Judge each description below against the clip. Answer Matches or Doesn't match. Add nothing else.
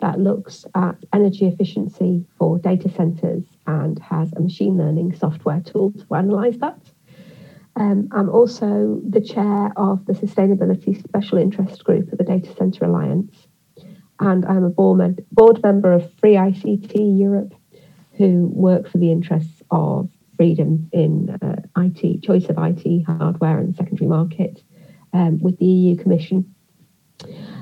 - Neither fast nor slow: Matches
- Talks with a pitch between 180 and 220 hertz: Matches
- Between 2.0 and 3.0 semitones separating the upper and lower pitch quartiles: Matches